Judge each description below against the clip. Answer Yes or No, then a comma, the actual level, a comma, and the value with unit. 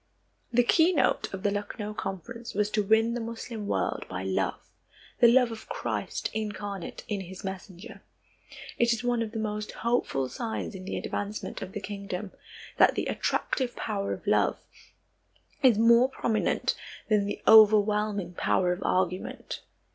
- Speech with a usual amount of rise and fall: Yes, average, 3.0 semitones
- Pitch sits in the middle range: No, high, 210 Hz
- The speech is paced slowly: No, average, 155 wpm